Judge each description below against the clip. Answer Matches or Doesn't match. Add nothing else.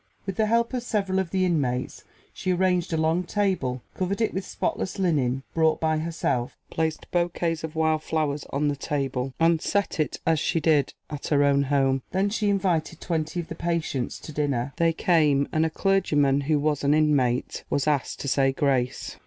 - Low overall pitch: Doesn't match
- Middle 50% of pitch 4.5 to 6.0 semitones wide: Doesn't match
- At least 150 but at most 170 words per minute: Doesn't match